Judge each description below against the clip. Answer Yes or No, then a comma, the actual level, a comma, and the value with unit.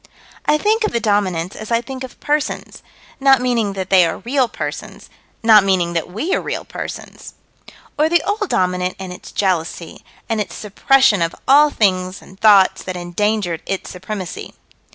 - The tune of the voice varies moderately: No, wide, 6.0 semitones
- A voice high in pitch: Yes, high, 205 Hz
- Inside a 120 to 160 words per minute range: No, average, 175 wpm